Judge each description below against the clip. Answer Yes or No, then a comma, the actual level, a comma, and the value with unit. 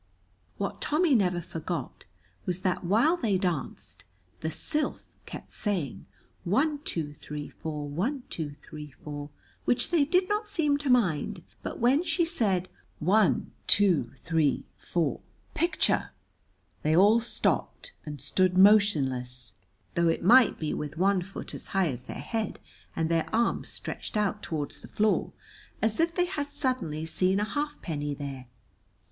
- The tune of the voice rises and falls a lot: Yes, wide, 8.2 semitones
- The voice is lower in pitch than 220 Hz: Yes, medium, 185 Hz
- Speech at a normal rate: Yes, average, 150 wpm